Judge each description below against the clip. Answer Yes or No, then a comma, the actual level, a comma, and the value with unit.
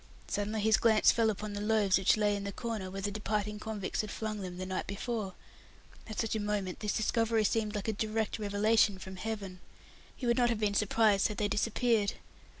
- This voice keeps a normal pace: No, fast, 215 wpm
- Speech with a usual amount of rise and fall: No, narrow, 1.6 semitones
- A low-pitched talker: No, high, 210 Hz